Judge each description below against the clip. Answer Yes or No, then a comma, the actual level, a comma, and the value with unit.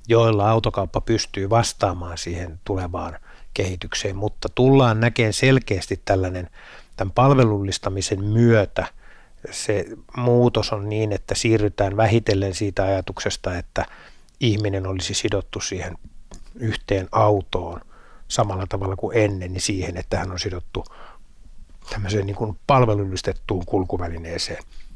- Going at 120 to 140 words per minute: No, average, 110 wpm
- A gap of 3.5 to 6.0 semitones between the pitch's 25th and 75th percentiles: No, average, 3.0 semitones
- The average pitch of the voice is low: Yes, low, 100 Hz